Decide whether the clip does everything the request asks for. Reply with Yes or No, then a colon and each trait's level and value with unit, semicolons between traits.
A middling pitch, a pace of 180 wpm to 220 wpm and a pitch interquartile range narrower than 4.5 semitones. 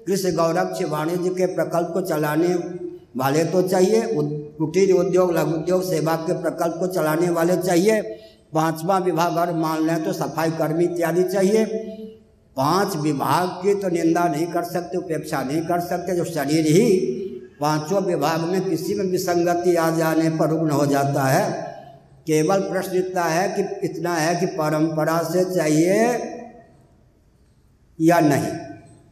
No: medium, 175 Hz; average, 150 wpm; narrow, 2.5 semitones